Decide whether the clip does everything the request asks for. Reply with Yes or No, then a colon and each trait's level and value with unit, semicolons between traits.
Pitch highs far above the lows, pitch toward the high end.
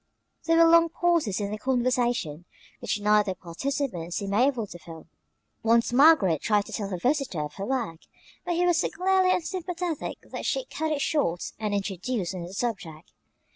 Yes: wide, 8.8 semitones; high, 230 Hz